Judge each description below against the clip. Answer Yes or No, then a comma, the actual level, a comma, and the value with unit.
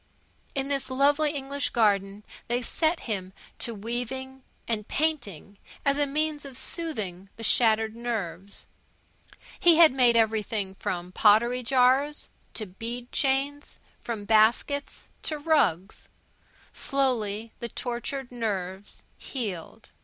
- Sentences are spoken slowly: Yes, slow, 115 wpm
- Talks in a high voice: Yes, high, 240 Hz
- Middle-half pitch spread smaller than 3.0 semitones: No, average, 4.9 semitones